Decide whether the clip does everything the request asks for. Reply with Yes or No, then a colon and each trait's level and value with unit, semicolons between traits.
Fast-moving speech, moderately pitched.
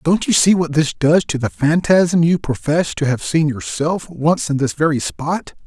Yes: fast, 210 wpm; medium, 155 Hz